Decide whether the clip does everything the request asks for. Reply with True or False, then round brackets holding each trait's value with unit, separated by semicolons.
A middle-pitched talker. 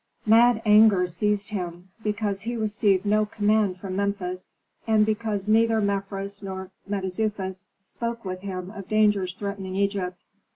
False (200 Hz)